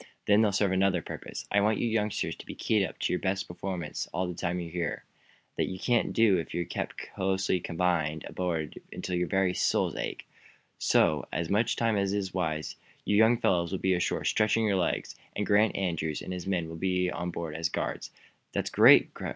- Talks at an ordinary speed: No, fast, 215 wpm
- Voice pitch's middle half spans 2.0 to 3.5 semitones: Yes, average, 2.8 semitones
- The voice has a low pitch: Yes, very low, 95 Hz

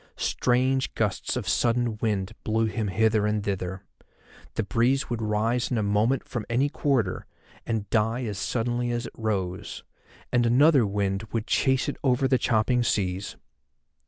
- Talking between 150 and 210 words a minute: Yes, average, 160 wpm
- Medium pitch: No, low, 115 Hz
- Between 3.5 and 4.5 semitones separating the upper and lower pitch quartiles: No, average, 2.9 semitones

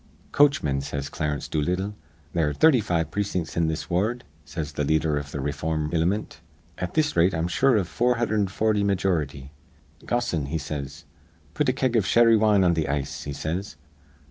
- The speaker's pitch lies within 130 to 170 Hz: No, very low, 85 Hz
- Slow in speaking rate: No, average, 170 wpm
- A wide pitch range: Yes, wide, 5.9 semitones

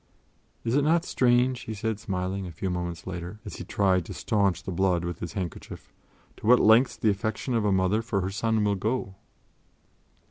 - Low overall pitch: Yes, low, 100 Hz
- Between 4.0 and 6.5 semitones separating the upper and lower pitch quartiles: No, average, 3.6 semitones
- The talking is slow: No, average, 200 wpm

